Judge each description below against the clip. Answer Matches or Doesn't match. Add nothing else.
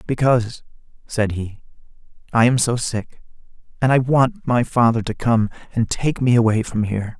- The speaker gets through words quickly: Doesn't match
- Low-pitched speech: Matches